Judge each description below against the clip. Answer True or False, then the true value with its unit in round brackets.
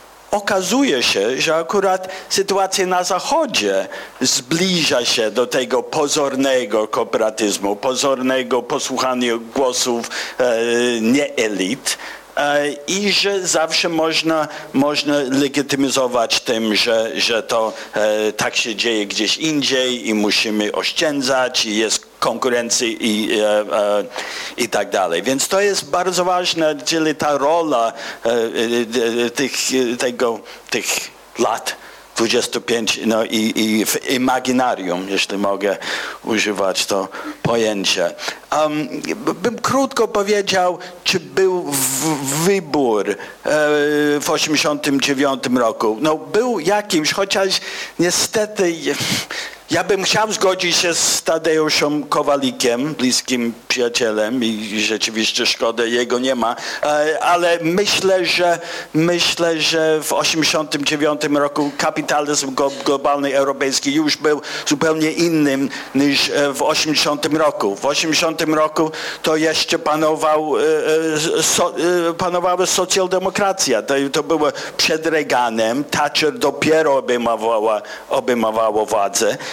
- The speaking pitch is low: False (150 Hz)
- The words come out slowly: True (105 wpm)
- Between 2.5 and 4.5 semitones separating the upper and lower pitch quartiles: False (5.4 semitones)